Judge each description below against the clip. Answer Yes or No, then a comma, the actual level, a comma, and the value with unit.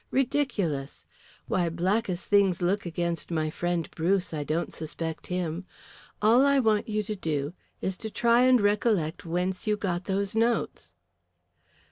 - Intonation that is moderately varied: Yes, average, 4.2 semitones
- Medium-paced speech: Yes, average, 150 wpm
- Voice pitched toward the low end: No, medium, 185 Hz